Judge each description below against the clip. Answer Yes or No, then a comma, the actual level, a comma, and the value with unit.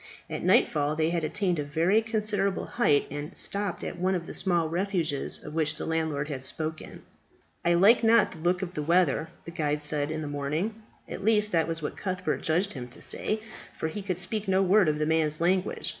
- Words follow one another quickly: Yes, fast, 215 wpm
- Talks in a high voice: No, medium, 170 Hz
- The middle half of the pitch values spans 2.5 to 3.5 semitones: No, average, 4.0 semitones